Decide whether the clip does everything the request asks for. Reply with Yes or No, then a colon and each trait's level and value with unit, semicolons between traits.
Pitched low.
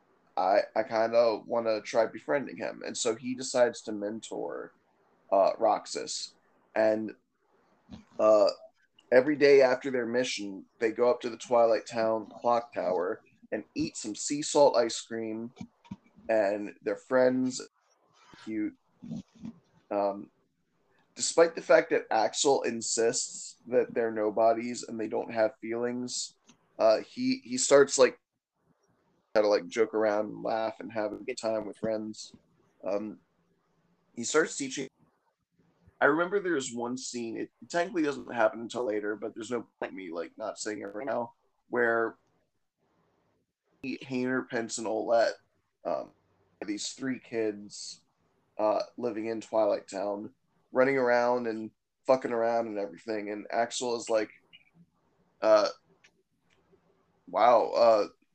Yes: low, 115 Hz